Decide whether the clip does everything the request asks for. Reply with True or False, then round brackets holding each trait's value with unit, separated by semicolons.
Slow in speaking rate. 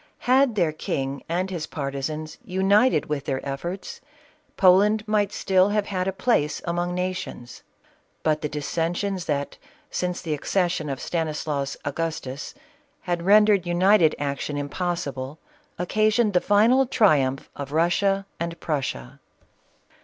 True (130 wpm)